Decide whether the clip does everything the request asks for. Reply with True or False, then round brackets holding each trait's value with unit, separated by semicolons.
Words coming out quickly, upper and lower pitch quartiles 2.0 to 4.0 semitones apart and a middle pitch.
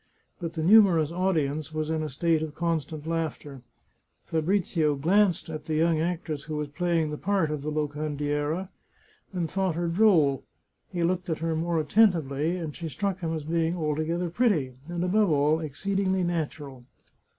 False (165 wpm; 2.6 semitones; 160 Hz)